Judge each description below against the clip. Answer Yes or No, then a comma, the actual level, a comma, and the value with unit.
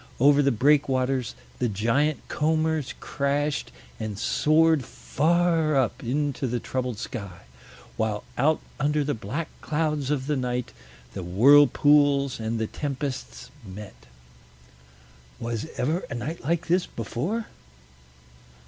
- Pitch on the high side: No, medium, 140 Hz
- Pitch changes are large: No, average, 4.2 semitones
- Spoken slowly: Yes, slow, 120 wpm